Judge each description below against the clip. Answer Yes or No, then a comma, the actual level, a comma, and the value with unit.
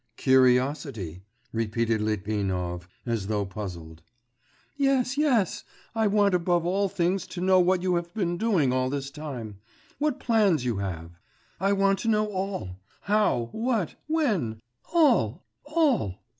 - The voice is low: No, medium, 170 Hz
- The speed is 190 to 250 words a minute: No, slow, 135 wpm